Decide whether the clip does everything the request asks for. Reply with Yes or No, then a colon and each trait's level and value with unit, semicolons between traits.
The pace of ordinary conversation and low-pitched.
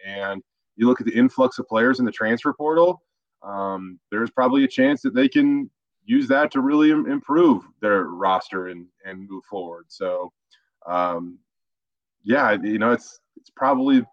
Yes: average, 165 wpm; low, 125 Hz